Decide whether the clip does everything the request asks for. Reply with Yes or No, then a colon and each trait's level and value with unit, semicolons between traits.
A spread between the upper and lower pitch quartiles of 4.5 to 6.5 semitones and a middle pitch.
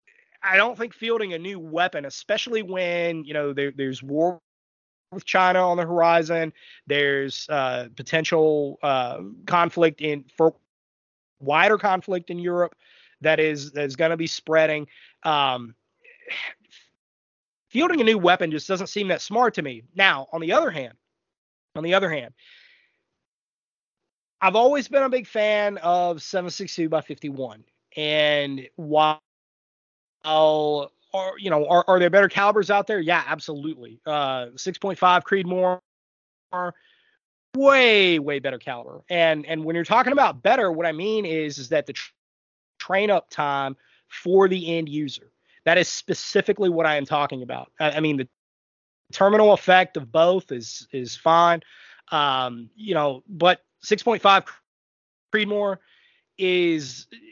Yes: average, 5.0 semitones; medium, 170 Hz